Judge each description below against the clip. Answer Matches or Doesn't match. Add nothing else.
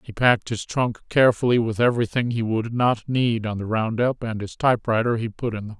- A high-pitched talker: Doesn't match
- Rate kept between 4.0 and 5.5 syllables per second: Doesn't match